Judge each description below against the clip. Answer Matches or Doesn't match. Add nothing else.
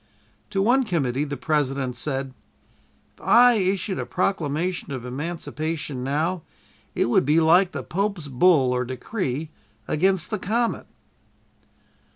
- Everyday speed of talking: Doesn't match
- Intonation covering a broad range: Matches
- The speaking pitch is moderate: Matches